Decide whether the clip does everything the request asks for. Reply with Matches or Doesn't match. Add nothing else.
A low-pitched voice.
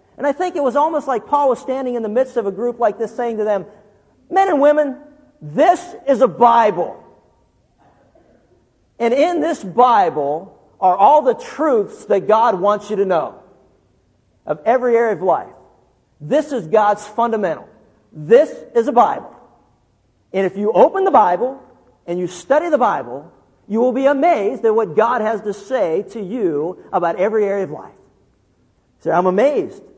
Doesn't match